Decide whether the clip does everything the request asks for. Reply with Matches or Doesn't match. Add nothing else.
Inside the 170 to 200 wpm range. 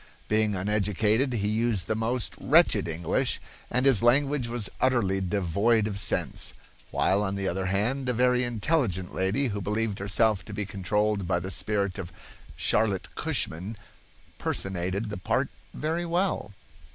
Doesn't match